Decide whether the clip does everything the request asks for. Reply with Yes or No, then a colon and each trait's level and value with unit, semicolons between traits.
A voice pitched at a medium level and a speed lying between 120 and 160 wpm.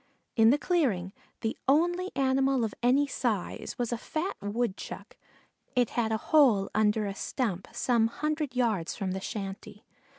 No: high, 235 Hz; average, 155 wpm